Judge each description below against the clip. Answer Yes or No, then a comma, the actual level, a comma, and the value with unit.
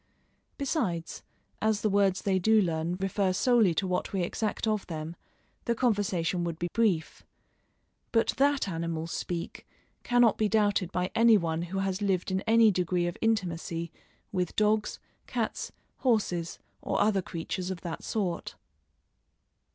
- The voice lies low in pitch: No, high, 190 Hz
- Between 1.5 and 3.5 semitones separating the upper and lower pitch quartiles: No, average, 3.9 semitones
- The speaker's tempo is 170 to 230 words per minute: No, average, 145 wpm